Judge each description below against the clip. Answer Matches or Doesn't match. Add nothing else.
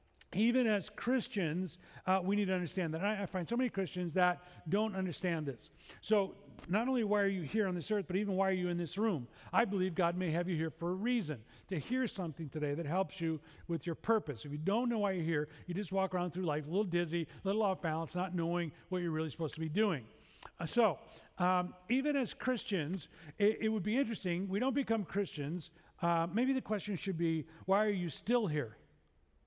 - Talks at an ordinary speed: Doesn't match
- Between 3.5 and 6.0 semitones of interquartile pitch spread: Matches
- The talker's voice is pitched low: Doesn't match